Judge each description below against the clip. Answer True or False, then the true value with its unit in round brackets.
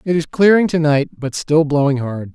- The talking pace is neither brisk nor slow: False (230 wpm)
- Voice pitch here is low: False (150 Hz)